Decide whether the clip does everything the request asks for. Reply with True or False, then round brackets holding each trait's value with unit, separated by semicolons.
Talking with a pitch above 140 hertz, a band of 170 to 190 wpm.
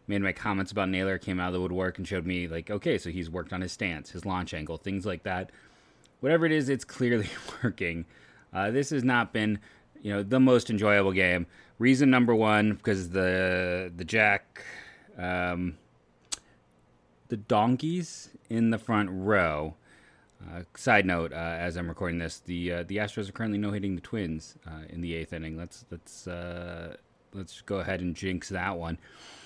False (95 Hz; 185 wpm)